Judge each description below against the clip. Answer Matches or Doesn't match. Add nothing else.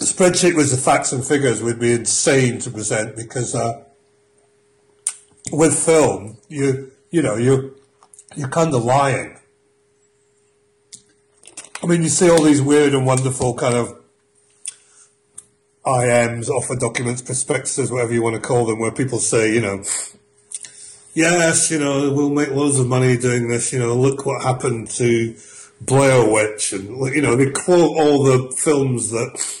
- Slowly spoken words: Doesn't match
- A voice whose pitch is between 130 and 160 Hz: Matches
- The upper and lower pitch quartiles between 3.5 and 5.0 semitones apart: Doesn't match